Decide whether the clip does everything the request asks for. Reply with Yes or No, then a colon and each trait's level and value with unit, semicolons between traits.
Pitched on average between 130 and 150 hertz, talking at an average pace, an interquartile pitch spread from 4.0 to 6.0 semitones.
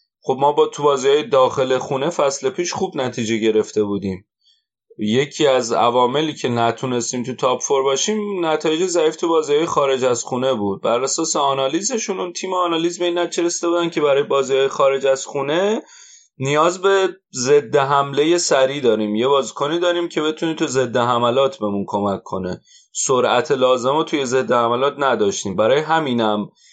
No: medium, 140 Hz; fast, 160 wpm; average, 5.2 semitones